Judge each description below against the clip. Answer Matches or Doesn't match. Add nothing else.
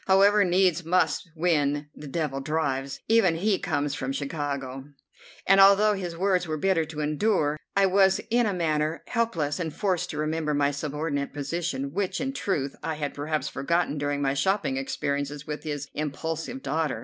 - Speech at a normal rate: Matches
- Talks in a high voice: Doesn't match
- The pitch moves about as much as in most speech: Matches